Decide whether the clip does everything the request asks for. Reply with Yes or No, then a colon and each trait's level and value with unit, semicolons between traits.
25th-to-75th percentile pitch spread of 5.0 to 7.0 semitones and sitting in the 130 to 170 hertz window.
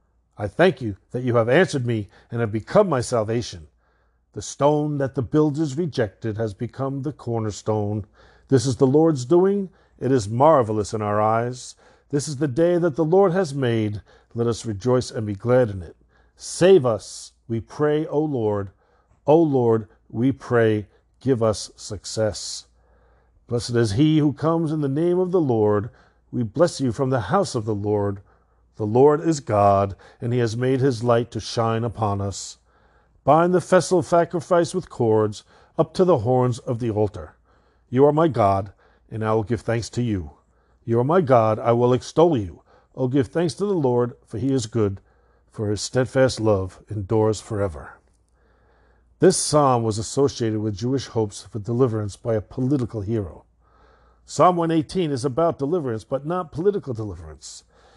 No: wide, 5.5 semitones; low, 120 Hz